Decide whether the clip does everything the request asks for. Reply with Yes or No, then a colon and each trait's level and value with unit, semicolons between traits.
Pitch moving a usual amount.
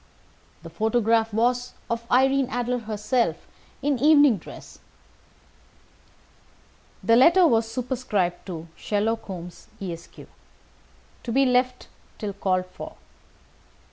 Yes: average, 3.9 semitones